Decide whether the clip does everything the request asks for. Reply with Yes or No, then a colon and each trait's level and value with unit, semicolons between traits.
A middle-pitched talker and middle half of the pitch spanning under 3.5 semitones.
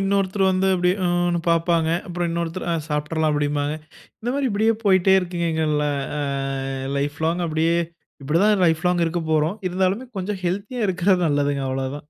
Yes: medium, 175 Hz; average, 3.0 semitones